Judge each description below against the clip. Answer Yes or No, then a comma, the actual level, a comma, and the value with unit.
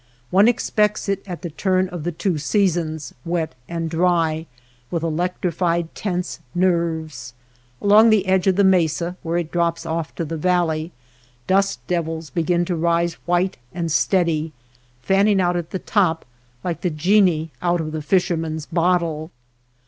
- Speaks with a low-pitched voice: No, medium, 170 Hz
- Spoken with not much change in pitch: Yes, narrow, 2.2 semitones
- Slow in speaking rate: No, average, 155 wpm